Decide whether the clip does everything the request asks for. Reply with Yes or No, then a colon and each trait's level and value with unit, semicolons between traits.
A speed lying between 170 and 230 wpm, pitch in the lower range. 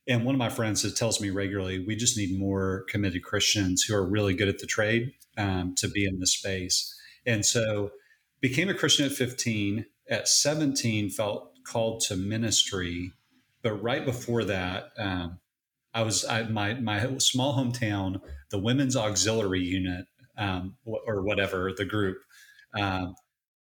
No: average, 160 wpm; low, 105 Hz